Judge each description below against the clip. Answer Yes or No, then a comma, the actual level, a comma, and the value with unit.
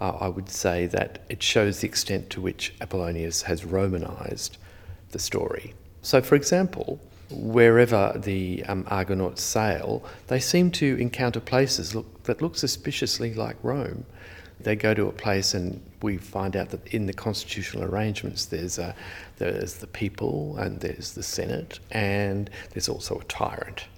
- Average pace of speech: Yes, average, 155 wpm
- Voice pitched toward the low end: Yes, low, 100 Hz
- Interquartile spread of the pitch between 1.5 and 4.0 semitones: Yes, average, 3.3 semitones